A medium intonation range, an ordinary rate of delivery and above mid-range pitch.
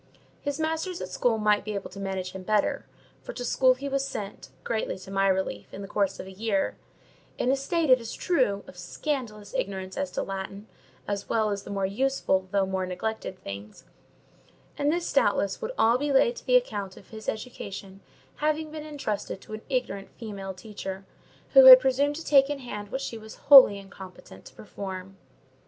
No: wide, 5.9 semitones; average, 195 wpm; high, 215 Hz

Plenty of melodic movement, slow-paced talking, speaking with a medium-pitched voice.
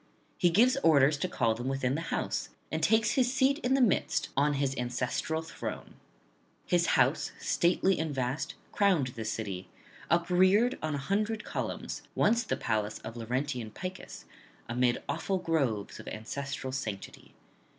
No: wide, 7.2 semitones; average, 150 wpm; medium, 145 Hz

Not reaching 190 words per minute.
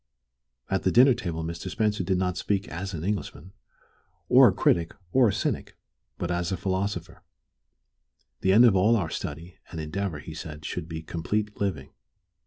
Yes: average, 170 wpm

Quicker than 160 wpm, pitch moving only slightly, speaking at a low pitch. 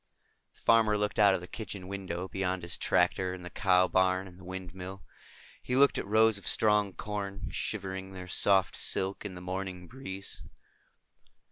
Yes: average, 170 wpm; narrow, 1.8 semitones; very low, 95 Hz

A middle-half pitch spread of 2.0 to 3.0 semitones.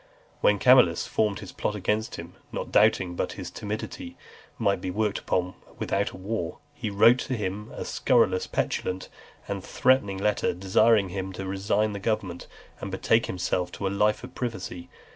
Yes: average, 2.7 semitones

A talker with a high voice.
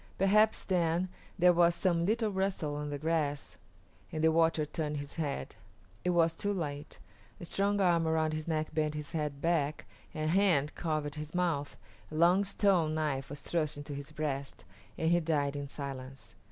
No: medium, 155 Hz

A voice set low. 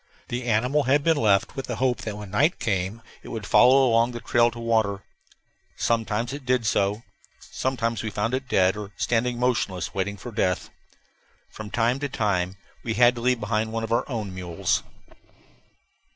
Yes: low, 115 Hz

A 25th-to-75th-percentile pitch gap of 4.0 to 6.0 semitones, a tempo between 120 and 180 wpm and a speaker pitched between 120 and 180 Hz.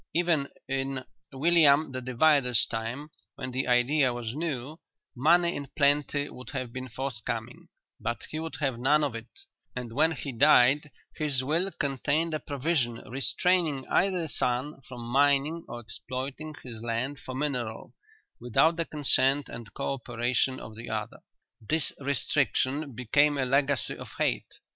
No: average, 3.3 semitones; average, 150 wpm; low, 135 Hz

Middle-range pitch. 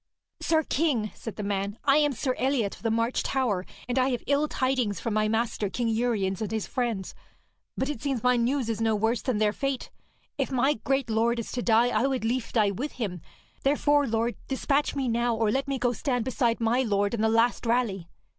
No: high, 235 Hz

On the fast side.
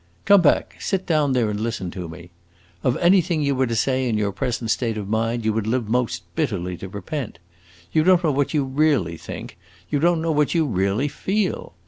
Yes: fast, 210 wpm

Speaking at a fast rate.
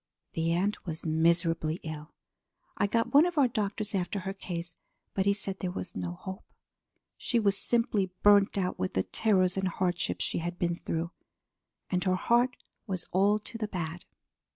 No: average, 175 wpm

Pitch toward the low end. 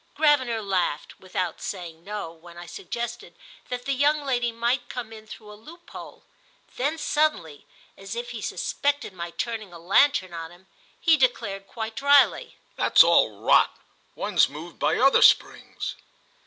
No: high, 225 Hz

